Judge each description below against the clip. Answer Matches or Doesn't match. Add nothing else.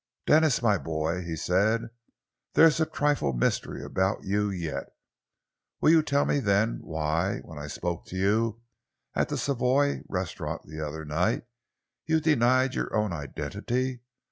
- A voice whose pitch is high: Doesn't match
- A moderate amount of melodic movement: Doesn't match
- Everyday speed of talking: Matches